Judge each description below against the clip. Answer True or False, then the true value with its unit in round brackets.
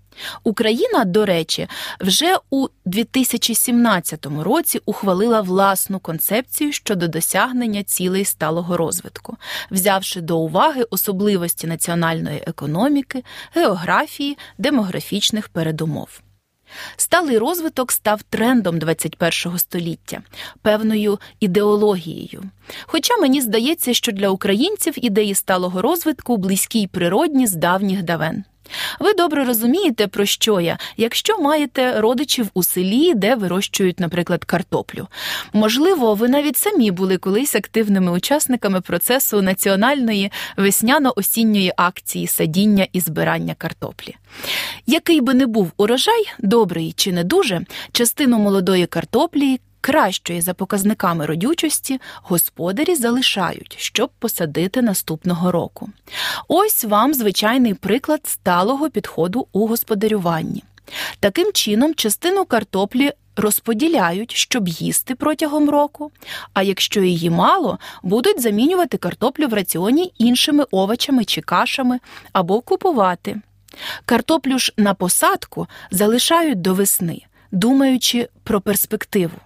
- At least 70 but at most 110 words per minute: True (105 wpm)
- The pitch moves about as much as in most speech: False (6.0 semitones)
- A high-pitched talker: True (215 Hz)